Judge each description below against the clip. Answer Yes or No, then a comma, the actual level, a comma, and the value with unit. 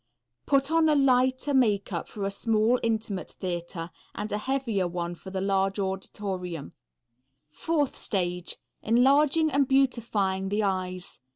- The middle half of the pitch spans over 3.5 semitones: Yes, wide, 5.6 semitones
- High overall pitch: Yes, high, 205 Hz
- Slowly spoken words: Yes, slow, 130 wpm